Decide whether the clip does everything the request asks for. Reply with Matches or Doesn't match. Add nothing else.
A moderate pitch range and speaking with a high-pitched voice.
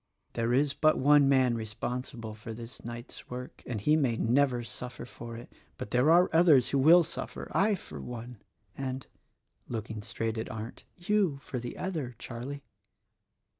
Doesn't match